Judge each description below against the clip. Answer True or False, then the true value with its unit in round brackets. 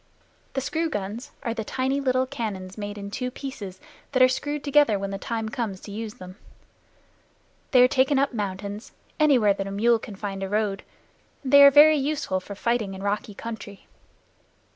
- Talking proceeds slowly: False (185 wpm)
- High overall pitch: True (225 Hz)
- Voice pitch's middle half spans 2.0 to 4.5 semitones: False (4.9 semitones)